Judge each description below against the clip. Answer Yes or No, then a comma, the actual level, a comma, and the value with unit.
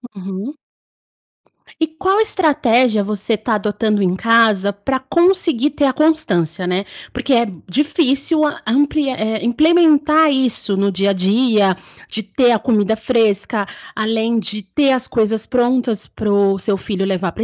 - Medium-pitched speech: No, high, 225 Hz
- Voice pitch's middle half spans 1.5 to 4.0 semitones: No, wide, 5.5 semitones